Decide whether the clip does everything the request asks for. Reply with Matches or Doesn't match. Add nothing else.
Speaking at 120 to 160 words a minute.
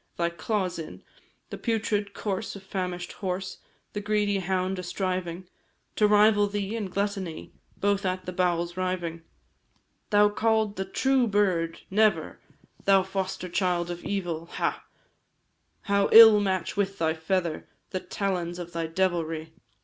Matches